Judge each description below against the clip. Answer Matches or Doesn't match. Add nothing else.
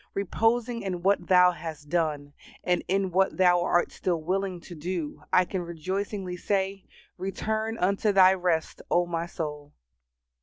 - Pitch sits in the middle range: Matches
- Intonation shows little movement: Matches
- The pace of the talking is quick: Doesn't match